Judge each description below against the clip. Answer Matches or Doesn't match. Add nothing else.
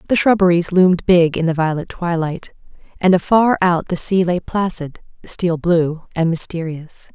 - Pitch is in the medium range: Matches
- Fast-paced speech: Doesn't match